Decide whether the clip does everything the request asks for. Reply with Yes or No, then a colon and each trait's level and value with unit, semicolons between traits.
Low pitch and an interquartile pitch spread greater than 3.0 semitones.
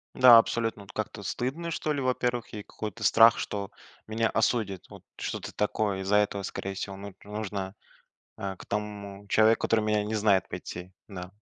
No: low, 105 Hz; narrow, 2.4 semitones